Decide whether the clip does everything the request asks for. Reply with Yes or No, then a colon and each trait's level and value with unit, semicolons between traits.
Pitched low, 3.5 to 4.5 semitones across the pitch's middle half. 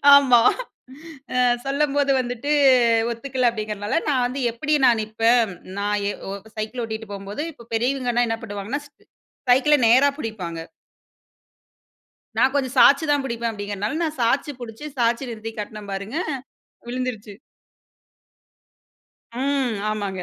No: high, 235 Hz; average, 4.1 semitones